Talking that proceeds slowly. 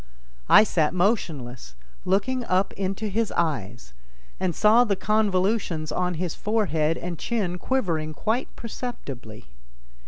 Yes: slow, 120 wpm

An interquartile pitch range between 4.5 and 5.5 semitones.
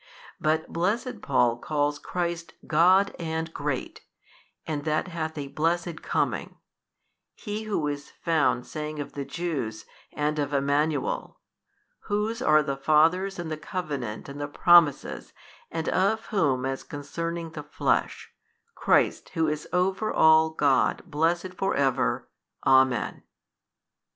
No: average, 3.2 semitones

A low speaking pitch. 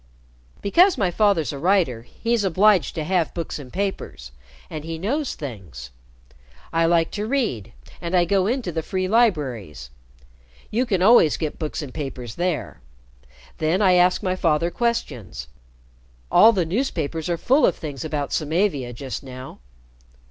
No: medium, 170 Hz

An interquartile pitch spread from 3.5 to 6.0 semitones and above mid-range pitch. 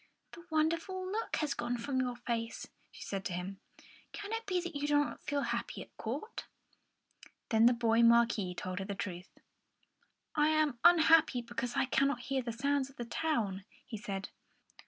Yes: average, 5.3 semitones; very high, 250 Hz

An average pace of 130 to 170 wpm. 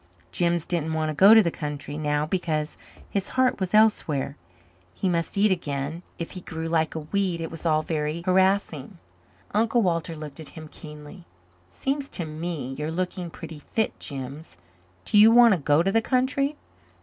No: average, 185 wpm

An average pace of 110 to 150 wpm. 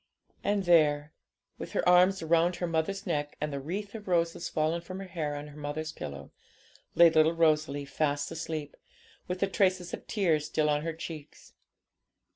No: average, 175 wpm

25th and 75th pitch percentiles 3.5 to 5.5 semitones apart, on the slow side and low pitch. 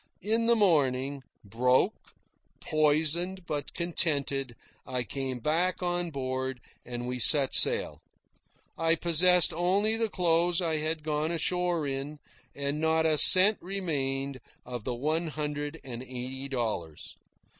No: average, 4.6 semitones; slow, 130 wpm; medium, 150 Hz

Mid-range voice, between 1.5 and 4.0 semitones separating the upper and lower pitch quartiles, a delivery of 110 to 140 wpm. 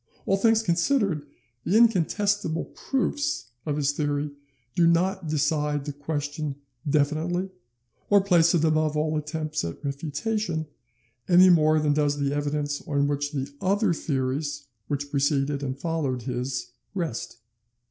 Yes: medium, 150 Hz; average, 3.3 semitones; slow, 135 wpm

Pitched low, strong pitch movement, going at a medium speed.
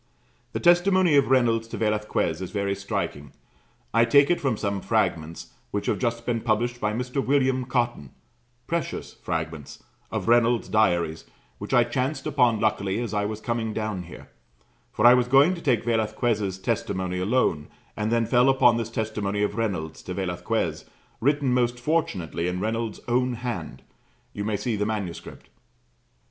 No: low, 115 Hz; average, 3.6 semitones; average, 160 wpm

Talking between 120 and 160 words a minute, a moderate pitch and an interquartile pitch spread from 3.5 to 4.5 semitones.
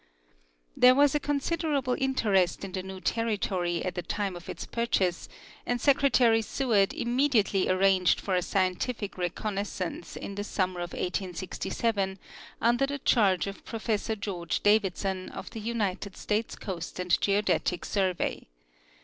No: average, 140 wpm; high, 200 Hz; average, 4.0 semitones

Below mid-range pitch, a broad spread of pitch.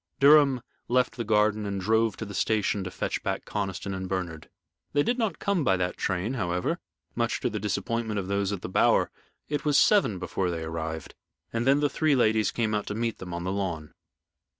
No: low, 105 Hz; average, 4.5 semitones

